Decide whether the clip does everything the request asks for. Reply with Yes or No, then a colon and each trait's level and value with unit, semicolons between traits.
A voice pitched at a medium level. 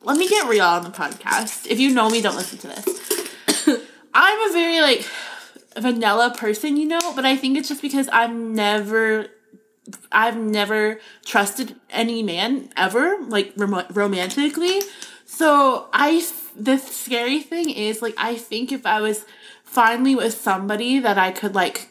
No: high, 235 Hz